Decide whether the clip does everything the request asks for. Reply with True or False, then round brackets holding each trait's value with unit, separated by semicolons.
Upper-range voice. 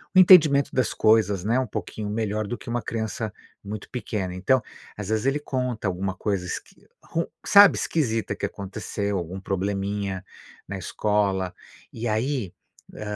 False (105 Hz)